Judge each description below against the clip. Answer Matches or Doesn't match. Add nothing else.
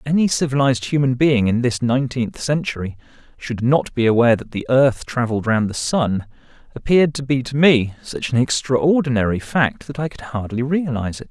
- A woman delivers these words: Doesn't match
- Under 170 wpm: Doesn't match